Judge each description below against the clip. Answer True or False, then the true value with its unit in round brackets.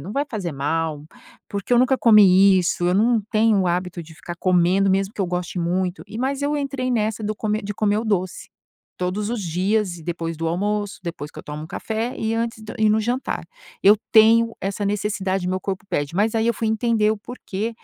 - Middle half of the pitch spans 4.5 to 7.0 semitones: False (3.6 semitones)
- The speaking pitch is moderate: False (205 Hz)